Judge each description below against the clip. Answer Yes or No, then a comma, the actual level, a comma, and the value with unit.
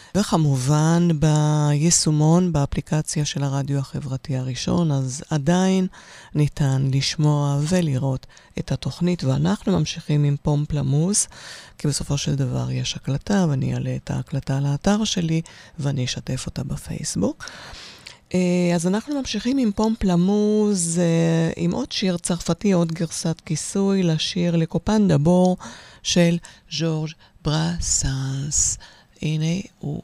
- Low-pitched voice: No, medium, 160 Hz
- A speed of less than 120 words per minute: Yes, average, 110 wpm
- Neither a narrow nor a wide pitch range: Yes, average, 3.9 semitones